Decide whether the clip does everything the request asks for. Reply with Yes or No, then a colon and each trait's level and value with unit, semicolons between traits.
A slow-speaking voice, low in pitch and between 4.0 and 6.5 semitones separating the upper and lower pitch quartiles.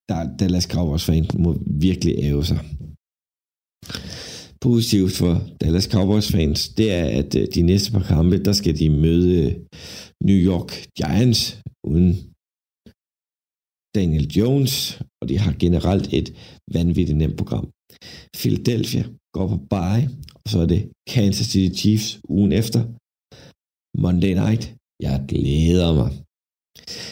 Yes: slow, 120 wpm; very low, 90 Hz; average, 4.3 semitones